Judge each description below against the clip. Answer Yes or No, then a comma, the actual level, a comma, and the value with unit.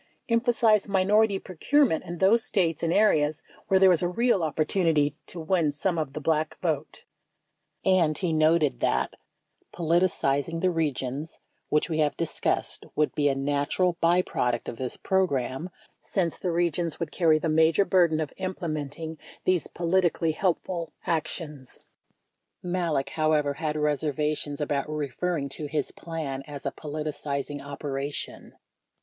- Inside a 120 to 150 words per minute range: Yes, average, 145 wpm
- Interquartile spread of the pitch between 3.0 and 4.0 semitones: Yes, average, 3.4 semitones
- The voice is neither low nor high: Yes, medium, 160 Hz